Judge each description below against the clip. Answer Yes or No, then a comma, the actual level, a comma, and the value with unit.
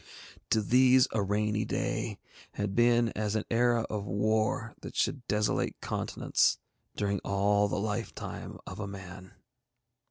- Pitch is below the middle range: Yes, low, 105 Hz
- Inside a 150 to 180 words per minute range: No, slow, 135 wpm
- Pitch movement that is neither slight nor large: No, narrow, 2.3 semitones